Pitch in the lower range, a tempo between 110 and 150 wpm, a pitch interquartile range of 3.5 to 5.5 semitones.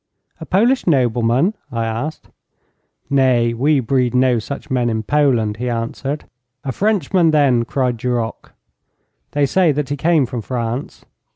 Yes: low, 130 Hz; average, 145 wpm; average, 3.9 semitones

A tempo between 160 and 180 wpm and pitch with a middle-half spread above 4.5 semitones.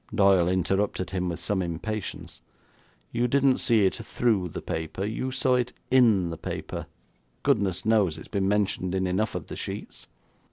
No: average, 165 wpm; average, 3.7 semitones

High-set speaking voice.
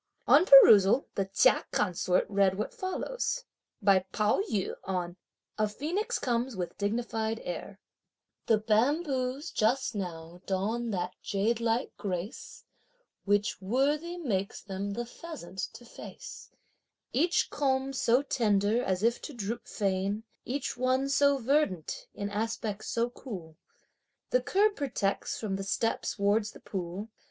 Yes: high, 220 Hz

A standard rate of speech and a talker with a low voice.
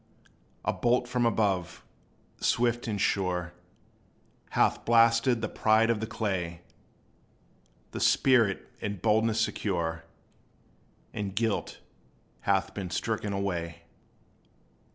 No: slow, 100 wpm; low, 105 Hz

